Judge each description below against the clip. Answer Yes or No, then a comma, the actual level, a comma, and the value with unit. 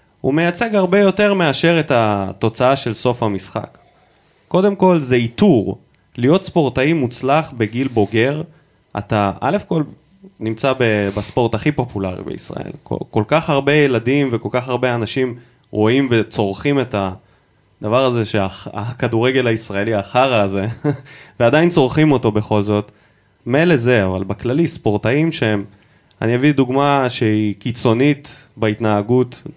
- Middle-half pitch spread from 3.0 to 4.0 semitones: No, average, 5.1 semitones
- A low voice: Yes, low, 125 Hz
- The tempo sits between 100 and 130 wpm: Yes, average, 125 wpm